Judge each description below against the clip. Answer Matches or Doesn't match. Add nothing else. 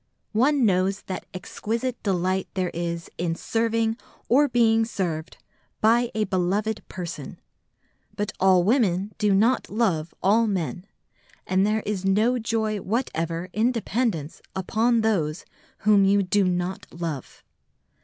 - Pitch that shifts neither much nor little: Matches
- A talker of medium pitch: Doesn't match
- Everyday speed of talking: Doesn't match